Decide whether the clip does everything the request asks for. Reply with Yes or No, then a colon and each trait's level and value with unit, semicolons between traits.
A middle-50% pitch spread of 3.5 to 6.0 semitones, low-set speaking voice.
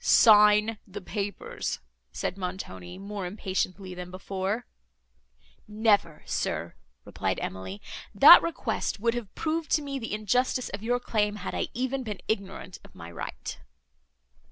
No: average, 3.8 semitones; high, 205 Hz